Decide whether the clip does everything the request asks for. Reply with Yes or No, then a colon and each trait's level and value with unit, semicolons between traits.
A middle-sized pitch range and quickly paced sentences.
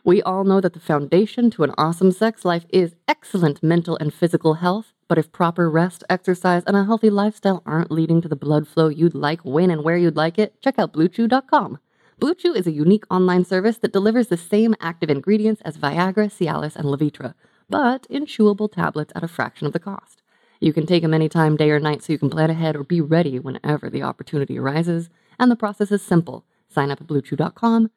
Yes: average, 4.7 semitones; fast, 210 wpm